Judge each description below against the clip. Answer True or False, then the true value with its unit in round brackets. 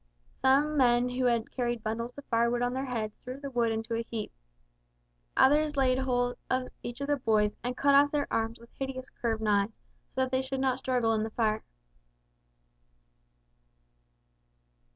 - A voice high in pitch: True (245 Hz)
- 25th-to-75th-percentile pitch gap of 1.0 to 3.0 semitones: True (2.5 semitones)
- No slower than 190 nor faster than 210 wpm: False (170 wpm)